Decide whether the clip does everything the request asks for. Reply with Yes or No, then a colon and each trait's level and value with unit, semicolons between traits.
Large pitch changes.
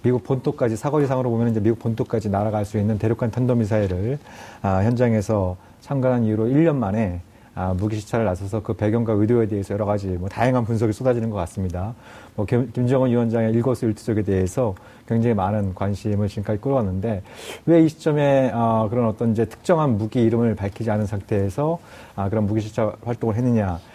No: average, 2.7 semitones